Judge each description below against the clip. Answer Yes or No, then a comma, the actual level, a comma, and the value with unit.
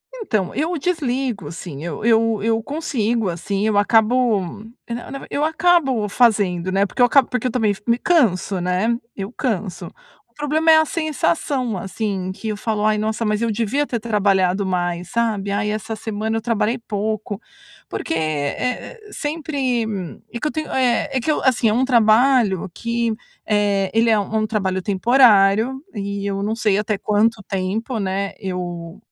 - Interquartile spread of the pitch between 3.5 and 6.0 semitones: Yes, average, 3.9 semitones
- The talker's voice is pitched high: Yes, high, 220 Hz